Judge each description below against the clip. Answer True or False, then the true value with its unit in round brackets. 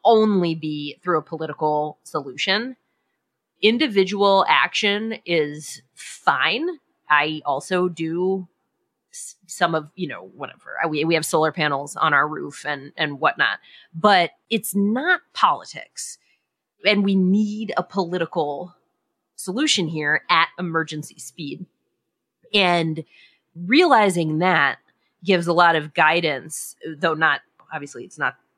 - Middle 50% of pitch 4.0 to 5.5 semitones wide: True (4.5 semitones)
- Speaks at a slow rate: True (120 wpm)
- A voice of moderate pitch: True (175 Hz)